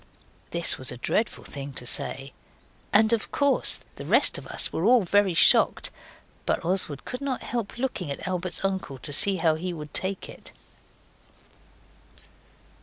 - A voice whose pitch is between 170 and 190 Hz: Yes, medium, 185 Hz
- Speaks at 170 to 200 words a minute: No, average, 160 wpm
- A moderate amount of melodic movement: No, wide, 6.2 semitones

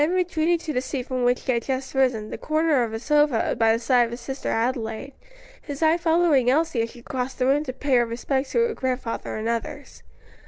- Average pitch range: Yes, average, 3.9 semitones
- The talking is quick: Yes, fast, 235 wpm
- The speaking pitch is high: Yes, very high, 260 Hz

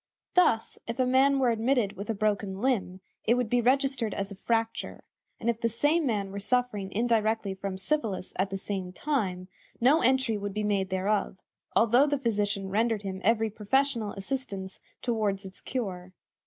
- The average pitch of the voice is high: Yes, high, 220 Hz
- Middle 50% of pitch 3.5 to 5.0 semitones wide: Yes, average, 4.1 semitones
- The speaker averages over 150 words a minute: Yes, average, 175 wpm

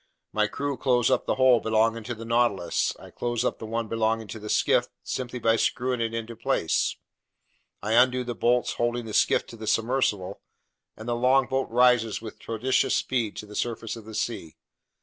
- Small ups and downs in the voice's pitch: Yes, narrow, 1.9 semitones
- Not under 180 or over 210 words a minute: Yes, average, 190 wpm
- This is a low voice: Yes, low, 115 Hz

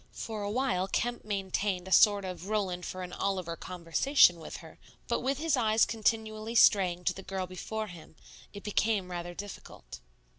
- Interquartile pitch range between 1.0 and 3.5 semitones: Yes, average, 3.2 semitones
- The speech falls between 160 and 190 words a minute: Yes, average, 175 wpm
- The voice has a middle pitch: No, high, 200 Hz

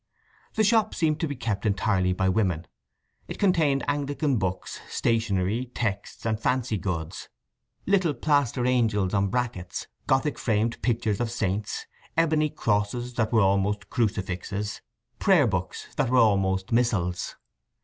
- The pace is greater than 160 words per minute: No, slow, 135 wpm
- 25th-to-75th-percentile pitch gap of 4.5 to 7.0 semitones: Yes, average, 5.2 semitones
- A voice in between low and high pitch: No, low, 110 Hz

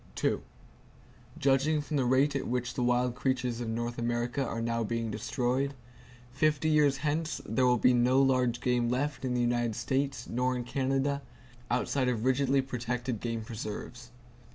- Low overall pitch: Yes, low, 125 Hz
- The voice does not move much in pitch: Yes, narrow, 2.2 semitones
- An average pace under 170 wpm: Yes, average, 160 wpm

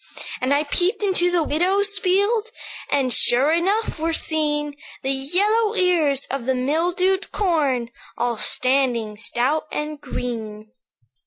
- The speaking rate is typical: No, slow, 130 wpm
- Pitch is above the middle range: Yes, very high, 300 Hz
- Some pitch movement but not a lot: No, wide, 6.0 semitones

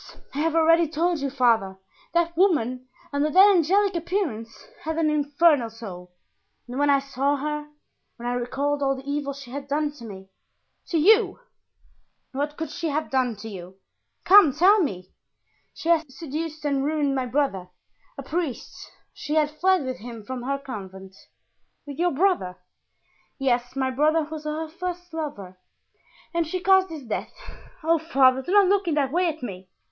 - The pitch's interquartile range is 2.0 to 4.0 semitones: No, average, 4.4 semitones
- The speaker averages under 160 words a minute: No, average, 175 wpm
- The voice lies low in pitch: No, very high, 290 Hz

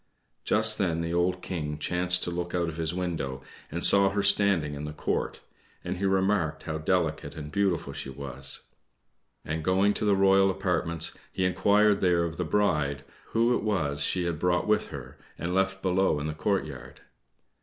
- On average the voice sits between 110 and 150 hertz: No, very low, 90 Hz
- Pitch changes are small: No, average, 3.6 semitones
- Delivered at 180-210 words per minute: Yes, average, 185 wpm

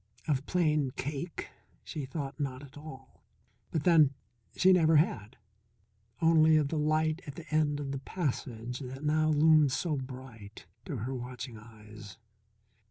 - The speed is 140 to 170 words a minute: Yes, average, 150 wpm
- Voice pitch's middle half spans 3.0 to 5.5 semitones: Yes, average, 3.3 semitones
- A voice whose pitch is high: No, medium, 145 Hz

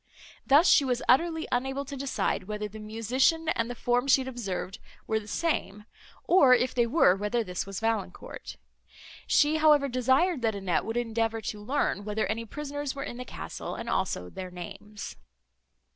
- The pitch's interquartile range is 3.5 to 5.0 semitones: Yes, average, 4.7 semitones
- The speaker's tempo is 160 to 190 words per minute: Yes, average, 175 wpm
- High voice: Yes, high, 240 Hz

